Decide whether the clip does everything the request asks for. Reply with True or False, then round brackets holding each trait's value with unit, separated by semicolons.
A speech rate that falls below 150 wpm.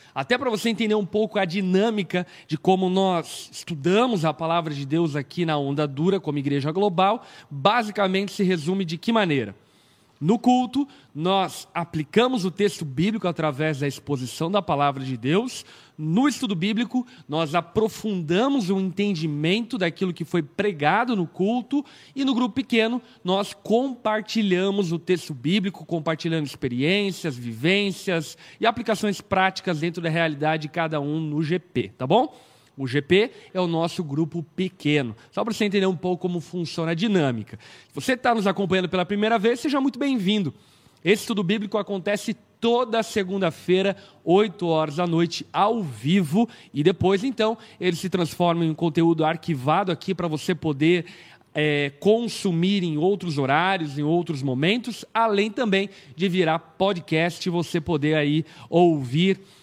False (155 wpm)